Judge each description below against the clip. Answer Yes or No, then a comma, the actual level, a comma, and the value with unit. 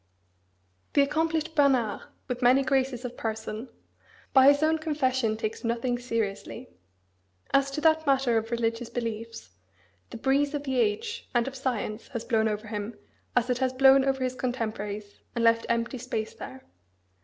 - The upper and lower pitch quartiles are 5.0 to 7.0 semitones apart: No, average, 3.2 semitones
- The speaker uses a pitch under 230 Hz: No, very high, 250 Hz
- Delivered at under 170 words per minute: Yes, average, 160 wpm